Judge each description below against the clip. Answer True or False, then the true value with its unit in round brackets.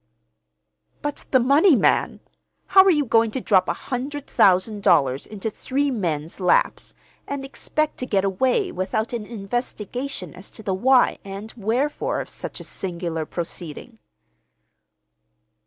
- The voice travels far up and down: True (6.2 semitones)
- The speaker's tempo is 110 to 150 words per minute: True (140 wpm)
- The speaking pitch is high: True (220 Hz)